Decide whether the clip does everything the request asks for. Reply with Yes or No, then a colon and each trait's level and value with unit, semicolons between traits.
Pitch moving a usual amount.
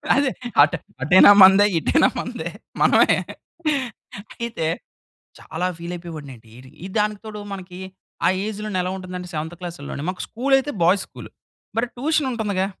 Yes: average, 4.0 semitones